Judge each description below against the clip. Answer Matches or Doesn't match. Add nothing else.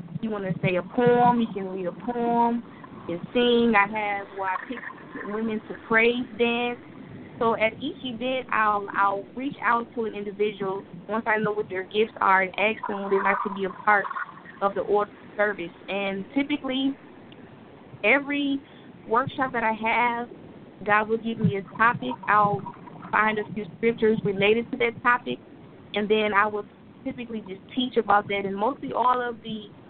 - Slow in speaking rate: Doesn't match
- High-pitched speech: Matches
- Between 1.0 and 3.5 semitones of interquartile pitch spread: Matches